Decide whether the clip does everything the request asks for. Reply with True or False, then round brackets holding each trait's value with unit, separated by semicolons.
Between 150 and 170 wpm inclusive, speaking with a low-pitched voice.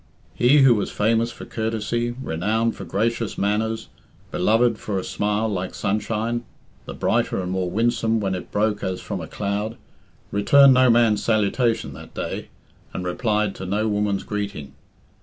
True (160 wpm; 105 Hz)